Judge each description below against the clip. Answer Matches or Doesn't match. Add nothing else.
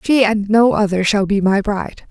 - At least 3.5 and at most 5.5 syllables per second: Matches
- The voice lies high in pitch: Matches